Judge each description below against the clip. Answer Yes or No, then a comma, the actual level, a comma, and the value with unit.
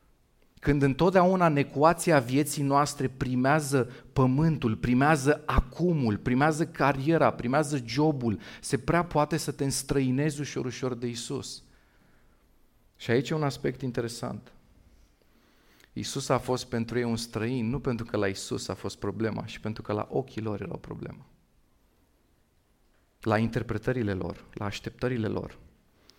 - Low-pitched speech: Yes, low, 130 Hz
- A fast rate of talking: No, average, 135 wpm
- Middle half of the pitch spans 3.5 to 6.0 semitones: Yes, average, 4.3 semitones